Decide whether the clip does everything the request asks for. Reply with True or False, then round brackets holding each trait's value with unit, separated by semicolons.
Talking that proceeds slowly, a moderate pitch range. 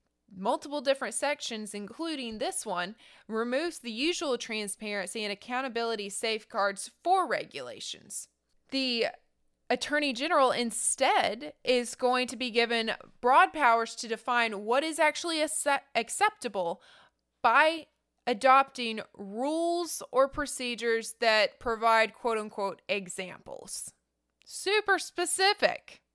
True (105 wpm; 5.0 semitones)